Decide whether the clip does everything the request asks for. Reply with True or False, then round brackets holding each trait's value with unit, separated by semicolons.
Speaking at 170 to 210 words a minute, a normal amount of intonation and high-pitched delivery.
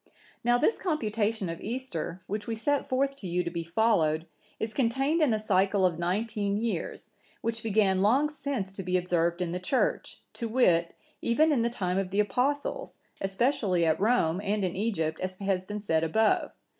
True (185 wpm; 4.5 semitones; 205 Hz)